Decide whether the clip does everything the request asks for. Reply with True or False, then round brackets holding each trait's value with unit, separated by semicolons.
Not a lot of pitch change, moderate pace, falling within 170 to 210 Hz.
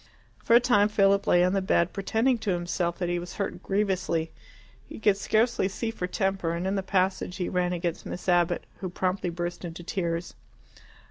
True (2.3 semitones; 195 wpm; 185 Hz)